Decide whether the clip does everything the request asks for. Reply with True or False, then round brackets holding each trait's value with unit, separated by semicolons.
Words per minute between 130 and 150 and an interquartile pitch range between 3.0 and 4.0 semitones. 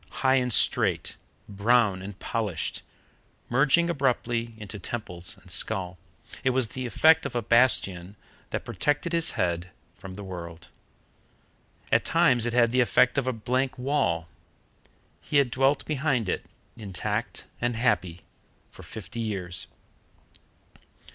False (135 wpm; 5.2 semitones)